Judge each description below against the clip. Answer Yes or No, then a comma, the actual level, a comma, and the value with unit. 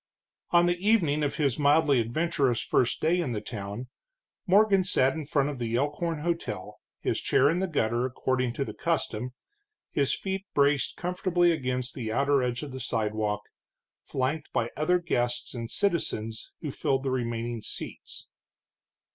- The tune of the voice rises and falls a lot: Yes, wide, 5.7 semitones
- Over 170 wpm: No, average, 160 wpm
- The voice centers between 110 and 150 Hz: Yes, medium, 140 Hz